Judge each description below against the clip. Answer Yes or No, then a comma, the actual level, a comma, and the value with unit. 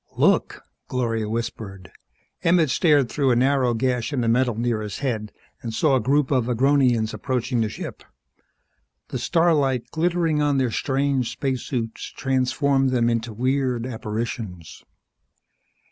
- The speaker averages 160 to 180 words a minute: No, slow, 135 wpm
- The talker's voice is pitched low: Yes, low, 125 Hz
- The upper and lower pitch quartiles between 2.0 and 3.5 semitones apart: Yes, average, 3.2 semitones